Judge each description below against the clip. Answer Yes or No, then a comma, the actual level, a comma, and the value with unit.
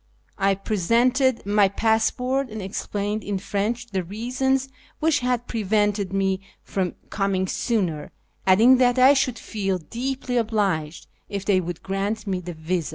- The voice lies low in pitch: No, high, 205 Hz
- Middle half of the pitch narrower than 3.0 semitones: No, average, 4.1 semitones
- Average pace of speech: Yes, average, 150 wpm